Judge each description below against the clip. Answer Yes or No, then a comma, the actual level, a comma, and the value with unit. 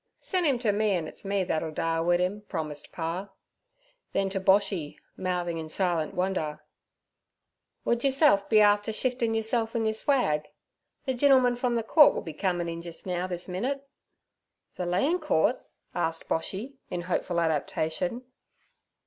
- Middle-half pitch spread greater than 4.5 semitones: Yes, wide, 5.4 semitones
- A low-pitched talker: No, high, 190 Hz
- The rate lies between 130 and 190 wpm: Yes, average, 155 wpm